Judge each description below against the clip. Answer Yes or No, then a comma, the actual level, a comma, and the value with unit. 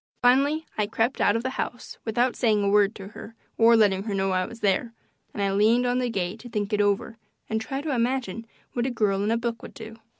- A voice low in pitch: No, high, 225 Hz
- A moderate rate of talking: No, fast, 245 wpm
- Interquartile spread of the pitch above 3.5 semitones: No, average, 3.0 semitones